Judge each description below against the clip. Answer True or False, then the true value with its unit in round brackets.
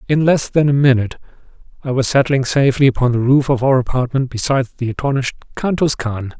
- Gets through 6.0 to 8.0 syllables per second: True (6.4 syllables/s)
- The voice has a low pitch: True (130 Hz)